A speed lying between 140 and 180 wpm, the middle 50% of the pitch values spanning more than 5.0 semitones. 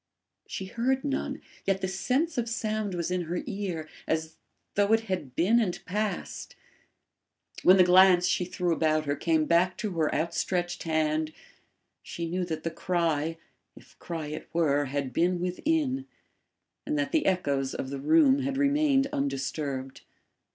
Yes: average, 160 wpm; wide, 5.5 semitones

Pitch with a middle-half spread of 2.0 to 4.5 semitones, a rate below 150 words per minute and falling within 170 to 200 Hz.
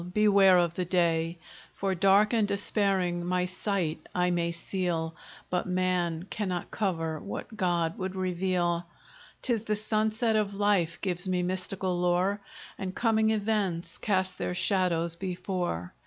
Yes: narrow, 2.5 semitones; average, 140 wpm; medium, 185 Hz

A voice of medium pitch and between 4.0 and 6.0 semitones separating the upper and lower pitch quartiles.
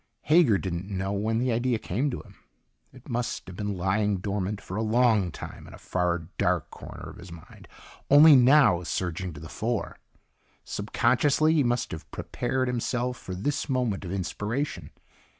No: low, 105 Hz; average, 5.2 semitones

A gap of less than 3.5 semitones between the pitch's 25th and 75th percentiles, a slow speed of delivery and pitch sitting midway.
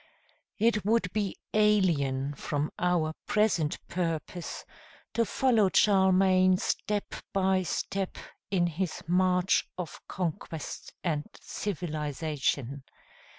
No: average, 4.0 semitones; slow, 95 wpm; medium, 180 Hz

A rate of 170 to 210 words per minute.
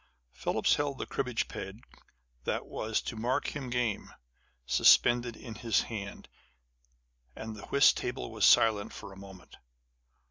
No: average, 140 wpm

